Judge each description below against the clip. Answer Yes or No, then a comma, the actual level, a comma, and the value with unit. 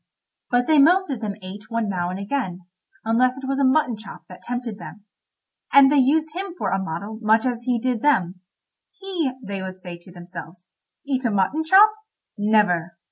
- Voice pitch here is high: Yes, high, 225 Hz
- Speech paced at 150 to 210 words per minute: Yes, average, 190 wpm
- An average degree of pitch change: No, wide, 6.4 semitones